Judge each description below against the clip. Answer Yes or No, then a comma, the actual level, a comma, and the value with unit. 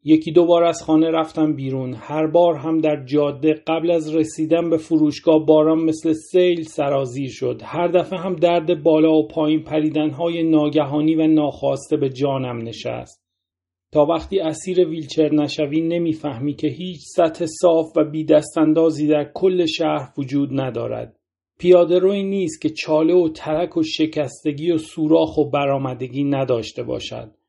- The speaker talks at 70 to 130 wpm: No, fast, 155 wpm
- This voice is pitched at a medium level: Yes, medium, 155 Hz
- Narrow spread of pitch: Yes, narrow, 1.9 semitones